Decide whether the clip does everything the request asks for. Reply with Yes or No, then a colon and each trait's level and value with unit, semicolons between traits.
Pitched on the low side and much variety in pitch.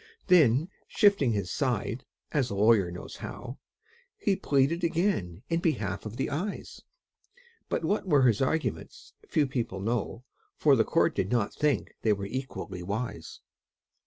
Yes: low, 125 Hz; wide, 7.4 semitones